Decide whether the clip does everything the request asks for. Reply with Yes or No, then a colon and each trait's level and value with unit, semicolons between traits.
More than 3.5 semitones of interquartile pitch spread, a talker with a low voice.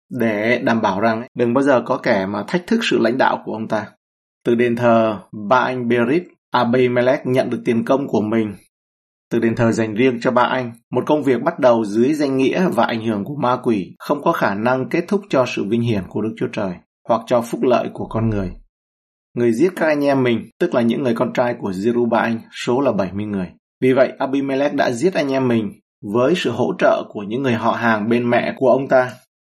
No: average, 2.7 semitones; low, 120 Hz